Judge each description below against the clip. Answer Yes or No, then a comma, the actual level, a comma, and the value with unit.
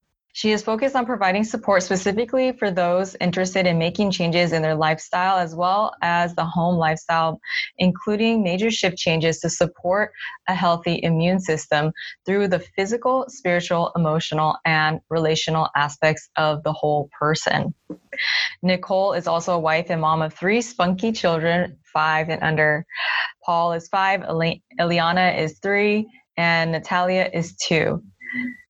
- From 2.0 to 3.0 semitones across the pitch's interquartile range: No, average, 3.4 semitones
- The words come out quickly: No, average, 140 wpm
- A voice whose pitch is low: No, medium, 175 Hz